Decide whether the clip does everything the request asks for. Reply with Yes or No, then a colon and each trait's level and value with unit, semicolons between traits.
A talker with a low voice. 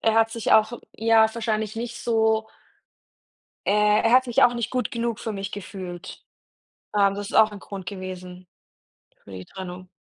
No: high, 215 Hz